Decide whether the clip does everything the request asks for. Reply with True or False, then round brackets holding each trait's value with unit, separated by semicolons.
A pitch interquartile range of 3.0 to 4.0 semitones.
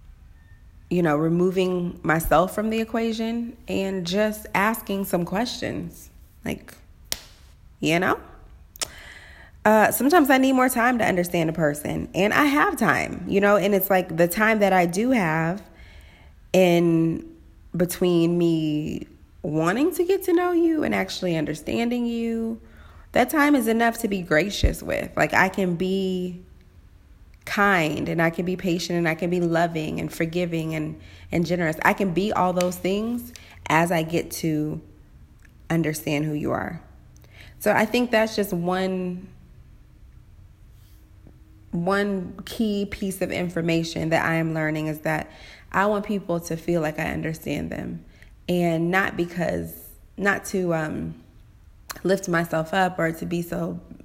False (4.4 semitones)